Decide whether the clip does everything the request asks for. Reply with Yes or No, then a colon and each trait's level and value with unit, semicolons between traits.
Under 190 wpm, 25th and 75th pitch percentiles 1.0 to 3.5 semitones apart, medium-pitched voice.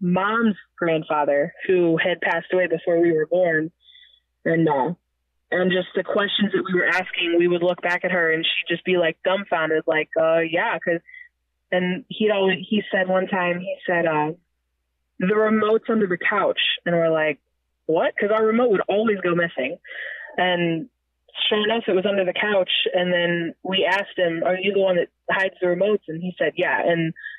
No: average, 195 wpm; average, 2.7 semitones; medium, 180 Hz